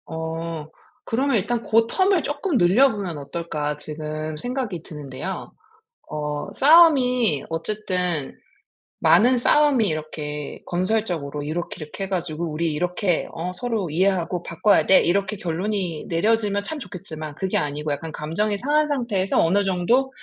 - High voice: No, medium, 180 Hz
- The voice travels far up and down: Yes, wide, 6.2 semitones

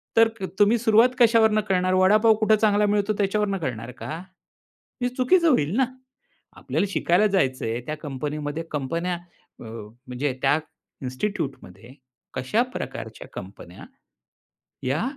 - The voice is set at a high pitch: No, medium, 180 Hz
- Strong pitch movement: Yes, wide, 8.4 semitones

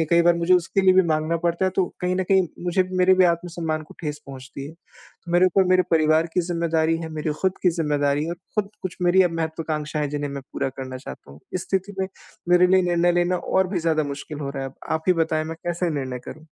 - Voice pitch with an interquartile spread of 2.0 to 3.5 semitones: Yes, average, 2.8 semitones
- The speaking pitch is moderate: Yes, medium, 170 Hz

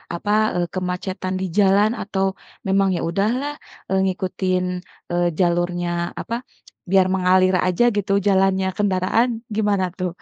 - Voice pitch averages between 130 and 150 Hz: No, high, 190 Hz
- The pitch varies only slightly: Yes, narrow, 1.6 semitones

